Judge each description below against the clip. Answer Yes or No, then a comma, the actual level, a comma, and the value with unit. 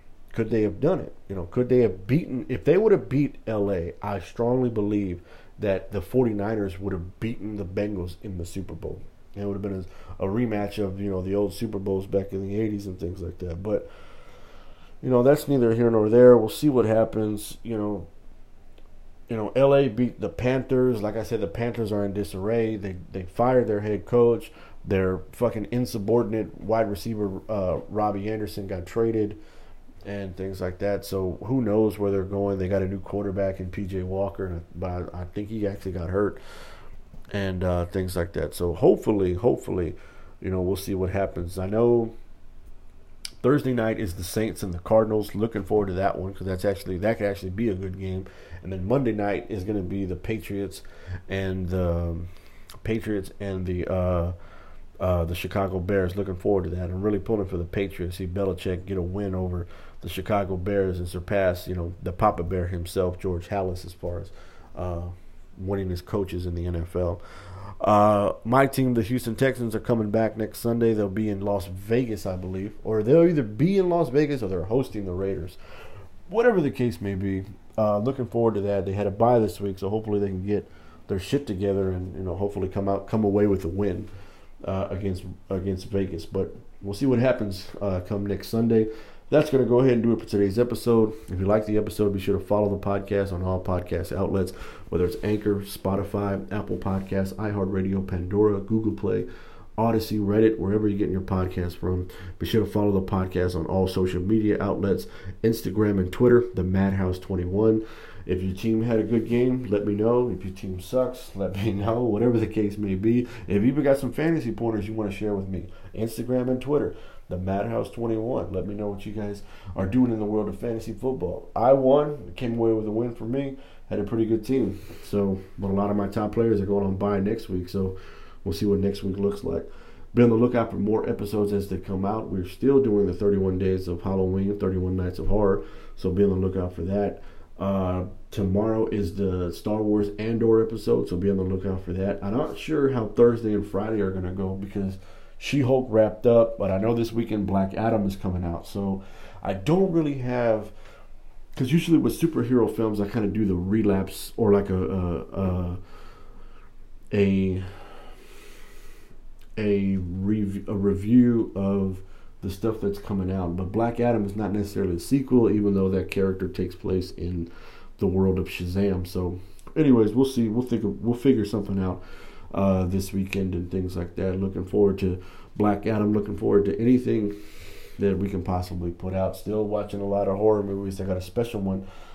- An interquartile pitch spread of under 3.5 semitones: Yes, average, 2.9 semitones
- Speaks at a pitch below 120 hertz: Yes, low, 100 Hz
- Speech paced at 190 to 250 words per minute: Yes, fast, 205 wpm